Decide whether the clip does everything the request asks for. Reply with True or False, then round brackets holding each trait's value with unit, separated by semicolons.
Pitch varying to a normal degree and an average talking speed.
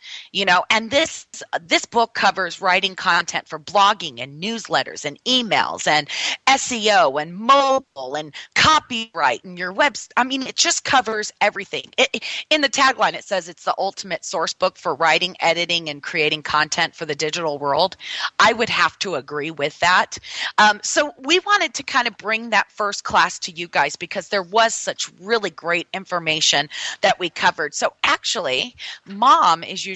False (6.3 semitones; 175 wpm)